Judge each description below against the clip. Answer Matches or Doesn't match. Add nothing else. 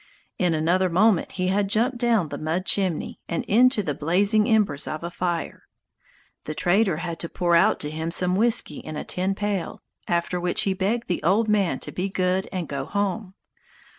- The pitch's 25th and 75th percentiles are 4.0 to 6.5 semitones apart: Doesn't match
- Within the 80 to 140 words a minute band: Doesn't match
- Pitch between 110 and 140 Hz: Doesn't match